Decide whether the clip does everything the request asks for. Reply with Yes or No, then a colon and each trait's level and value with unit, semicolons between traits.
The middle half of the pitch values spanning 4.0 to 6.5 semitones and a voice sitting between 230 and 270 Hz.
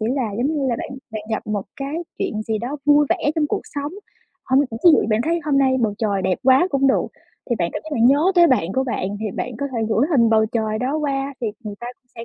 Yes: average, 4.3 semitones; very high, 255 Hz